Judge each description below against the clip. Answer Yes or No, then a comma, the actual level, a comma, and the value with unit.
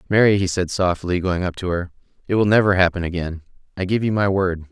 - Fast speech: Yes, fast, 230 wpm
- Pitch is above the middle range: No, very low, 95 Hz